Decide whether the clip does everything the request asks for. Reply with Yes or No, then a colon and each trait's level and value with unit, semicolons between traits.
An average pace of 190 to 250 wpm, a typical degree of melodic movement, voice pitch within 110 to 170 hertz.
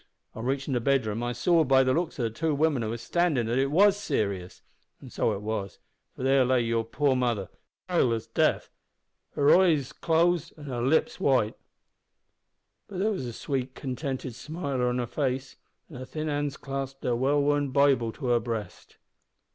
Yes: average, 195 wpm; average, 3.5 semitones; low, 135 Hz